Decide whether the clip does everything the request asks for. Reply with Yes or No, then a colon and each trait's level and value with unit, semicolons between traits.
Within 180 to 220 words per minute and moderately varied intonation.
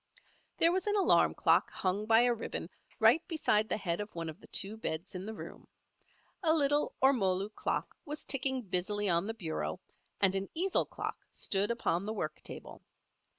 No: average, 185 wpm; wide, 6.0 semitones